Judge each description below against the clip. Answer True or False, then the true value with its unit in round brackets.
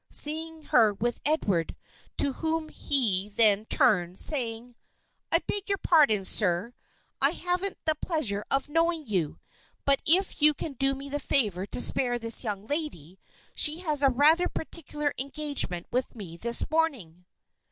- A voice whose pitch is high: True (270 Hz)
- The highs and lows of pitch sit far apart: True (6.8 semitones)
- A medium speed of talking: True (150 wpm)